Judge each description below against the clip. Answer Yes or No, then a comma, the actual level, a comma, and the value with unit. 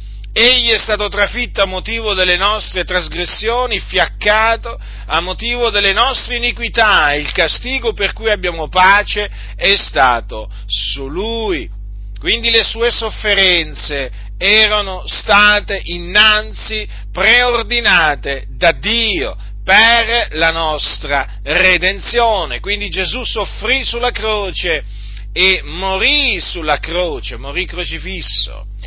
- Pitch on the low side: No, high, 195 Hz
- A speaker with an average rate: No, slow, 105 wpm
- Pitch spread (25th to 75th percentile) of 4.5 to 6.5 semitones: Yes, wide, 5.6 semitones